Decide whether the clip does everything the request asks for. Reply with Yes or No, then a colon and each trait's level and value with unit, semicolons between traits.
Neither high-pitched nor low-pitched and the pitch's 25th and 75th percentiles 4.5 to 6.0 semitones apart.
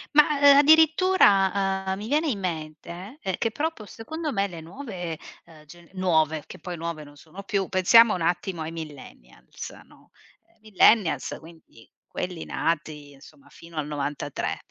Yes: medium, 180 Hz; wide, 5.6 semitones